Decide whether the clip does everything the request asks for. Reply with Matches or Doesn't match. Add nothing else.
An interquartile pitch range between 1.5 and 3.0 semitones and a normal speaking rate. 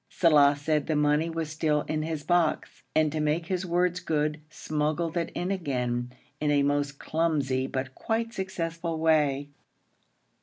Matches